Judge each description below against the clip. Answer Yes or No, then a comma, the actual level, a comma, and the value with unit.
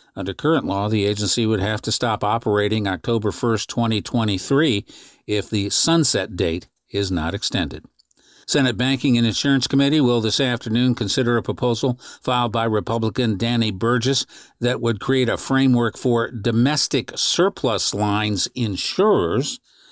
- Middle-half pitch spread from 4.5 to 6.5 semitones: No, average, 3.0 semitones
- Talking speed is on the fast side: No, average, 140 wpm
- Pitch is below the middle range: Yes, low, 115 Hz